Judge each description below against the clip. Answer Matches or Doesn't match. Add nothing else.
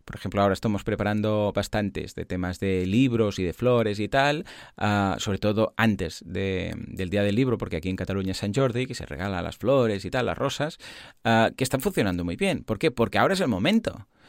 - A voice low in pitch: Matches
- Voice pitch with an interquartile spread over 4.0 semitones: Doesn't match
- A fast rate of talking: Matches